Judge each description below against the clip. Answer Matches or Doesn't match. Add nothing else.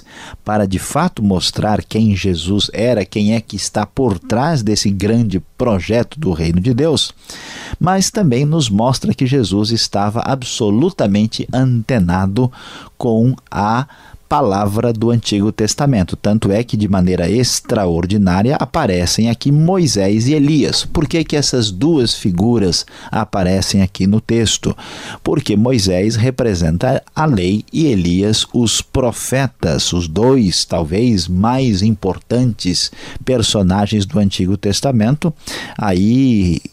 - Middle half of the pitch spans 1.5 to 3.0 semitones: Doesn't match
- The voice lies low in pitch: Matches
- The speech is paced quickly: Doesn't match